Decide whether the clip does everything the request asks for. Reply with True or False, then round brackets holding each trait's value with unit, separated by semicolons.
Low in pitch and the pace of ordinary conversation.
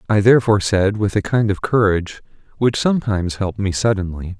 True (105 Hz; 190 wpm)